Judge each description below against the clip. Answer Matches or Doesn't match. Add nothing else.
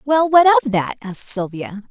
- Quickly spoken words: Doesn't match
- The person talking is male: Doesn't match